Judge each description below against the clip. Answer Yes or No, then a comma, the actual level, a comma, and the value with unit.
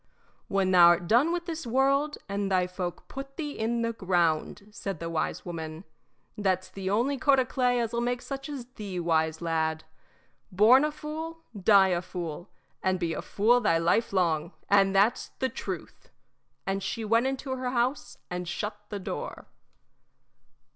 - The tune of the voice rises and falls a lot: Yes, wide, 6.2 semitones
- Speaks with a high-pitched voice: Yes, high, 205 Hz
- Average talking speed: Yes, average, 175 wpm